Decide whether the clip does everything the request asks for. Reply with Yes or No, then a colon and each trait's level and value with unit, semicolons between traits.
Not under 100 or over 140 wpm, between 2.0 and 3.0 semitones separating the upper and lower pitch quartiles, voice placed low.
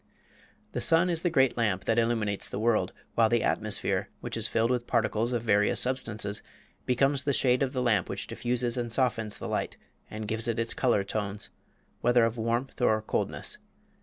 No: average, 190 wpm; narrow, 2.4 semitones; low, 115 Hz